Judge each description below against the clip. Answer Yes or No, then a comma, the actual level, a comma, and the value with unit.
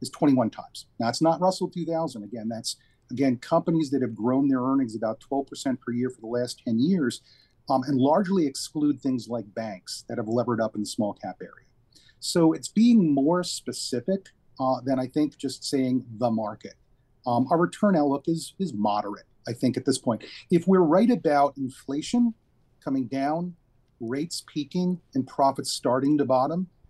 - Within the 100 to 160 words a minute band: No, average, 180 wpm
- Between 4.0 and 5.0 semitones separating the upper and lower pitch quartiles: Yes, average, 4.3 semitones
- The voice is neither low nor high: No, low, 130 Hz